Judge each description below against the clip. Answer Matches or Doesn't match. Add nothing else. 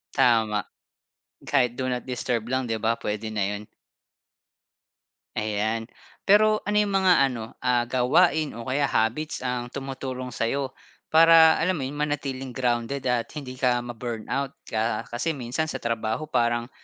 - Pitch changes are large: Doesn't match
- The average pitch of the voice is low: Matches